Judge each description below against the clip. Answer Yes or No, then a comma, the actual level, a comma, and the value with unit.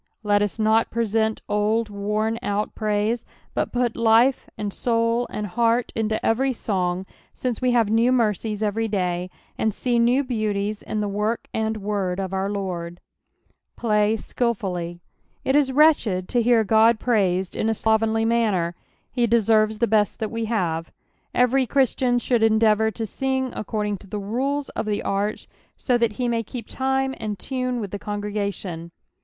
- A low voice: No, high, 220 Hz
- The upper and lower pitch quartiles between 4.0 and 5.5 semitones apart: No, narrow, 2.5 semitones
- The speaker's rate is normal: Yes, average, 170 wpm